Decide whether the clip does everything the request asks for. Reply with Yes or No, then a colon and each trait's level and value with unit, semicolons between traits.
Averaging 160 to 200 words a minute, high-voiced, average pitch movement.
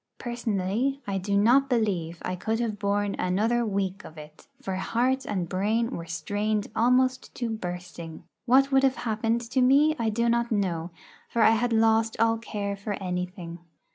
Yes: average, 170 wpm; high, 220 Hz; average, 3.9 semitones